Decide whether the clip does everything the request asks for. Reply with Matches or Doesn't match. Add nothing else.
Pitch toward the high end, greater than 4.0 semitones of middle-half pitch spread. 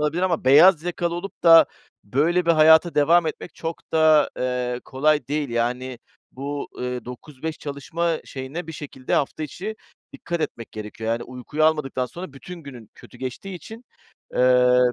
Doesn't match